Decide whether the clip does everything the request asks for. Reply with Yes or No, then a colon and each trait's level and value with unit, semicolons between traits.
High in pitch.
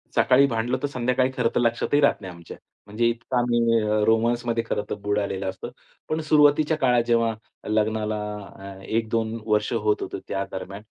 No: low, 115 Hz